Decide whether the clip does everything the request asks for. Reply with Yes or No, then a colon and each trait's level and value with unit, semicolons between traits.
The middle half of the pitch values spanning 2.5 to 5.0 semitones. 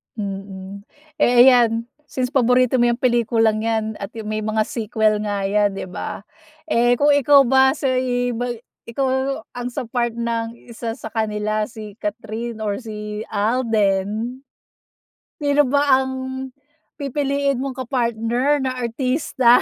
Yes: average, 3.1 semitones